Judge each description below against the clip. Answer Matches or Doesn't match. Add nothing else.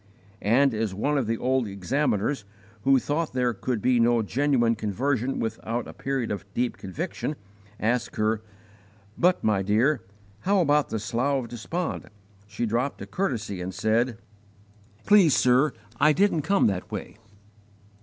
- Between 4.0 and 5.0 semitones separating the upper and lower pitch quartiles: Matches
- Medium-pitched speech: Doesn't match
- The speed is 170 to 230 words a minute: Doesn't match